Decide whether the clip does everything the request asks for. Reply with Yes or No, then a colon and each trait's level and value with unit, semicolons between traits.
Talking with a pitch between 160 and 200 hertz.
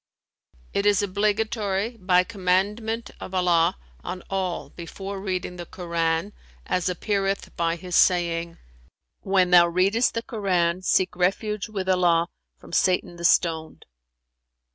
Yes: medium, 185 Hz